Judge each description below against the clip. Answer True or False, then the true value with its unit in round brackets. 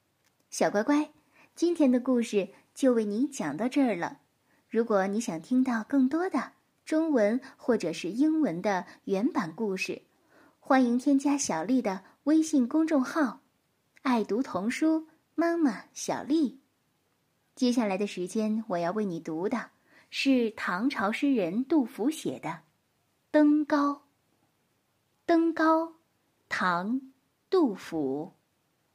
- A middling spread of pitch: False (6.1 semitones)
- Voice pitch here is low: False (260 Hz)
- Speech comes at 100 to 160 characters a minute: False (175 characters per minute)